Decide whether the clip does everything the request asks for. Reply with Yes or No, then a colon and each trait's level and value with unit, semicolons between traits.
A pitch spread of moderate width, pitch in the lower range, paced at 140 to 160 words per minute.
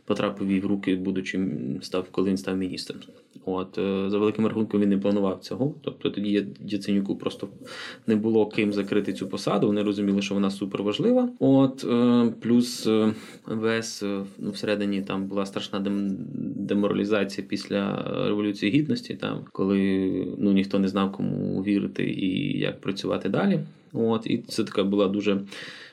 No: narrow, 1.7 semitones; low, 100 Hz; average, 150 wpm